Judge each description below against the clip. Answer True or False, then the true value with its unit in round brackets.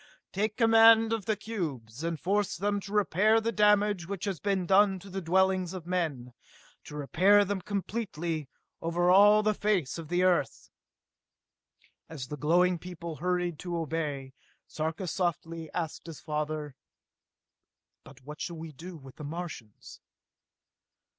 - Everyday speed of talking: True (145 wpm)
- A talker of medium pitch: True (175 Hz)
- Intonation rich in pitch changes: False (4.1 semitones)